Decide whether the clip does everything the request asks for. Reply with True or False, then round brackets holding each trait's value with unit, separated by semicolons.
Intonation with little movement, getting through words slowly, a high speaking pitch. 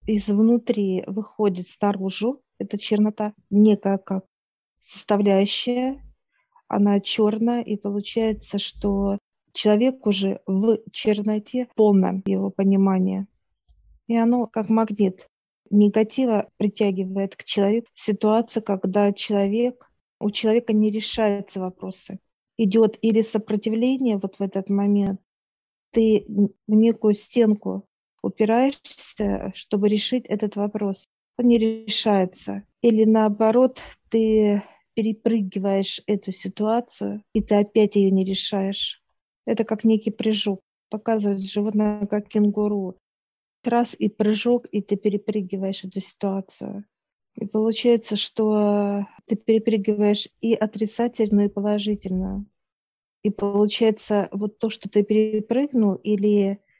True (1.8 semitones; 105 wpm; 210 Hz)